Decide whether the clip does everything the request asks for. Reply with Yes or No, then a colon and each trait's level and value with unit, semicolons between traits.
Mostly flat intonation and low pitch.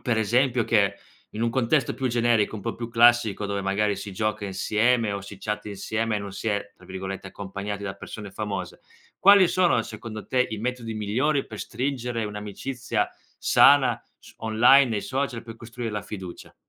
No: average, 3.0 semitones; low, 110 Hz